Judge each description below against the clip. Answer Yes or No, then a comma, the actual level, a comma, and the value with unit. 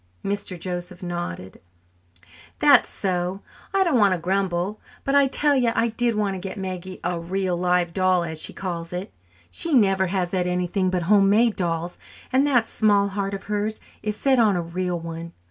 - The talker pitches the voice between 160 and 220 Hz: Yes, high, 190 Hz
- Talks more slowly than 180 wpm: No, average, 185 wpm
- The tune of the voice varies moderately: Yes, average, 3.0 semitones